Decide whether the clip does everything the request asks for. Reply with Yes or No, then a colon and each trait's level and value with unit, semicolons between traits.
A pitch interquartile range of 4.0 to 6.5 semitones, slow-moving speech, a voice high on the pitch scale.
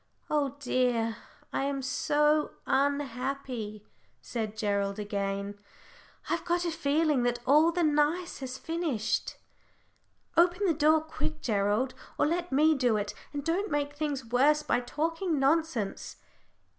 Yes: average, 4.8 semitones; slow, 130 wpm; very high, 280 Hz